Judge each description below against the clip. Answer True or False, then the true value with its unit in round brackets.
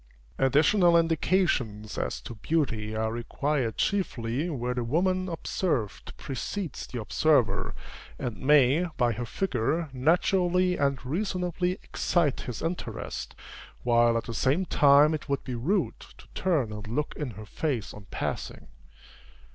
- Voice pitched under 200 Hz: True (140 Hz)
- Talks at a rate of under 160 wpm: True (135 wpm)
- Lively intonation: True (6.5 semitones)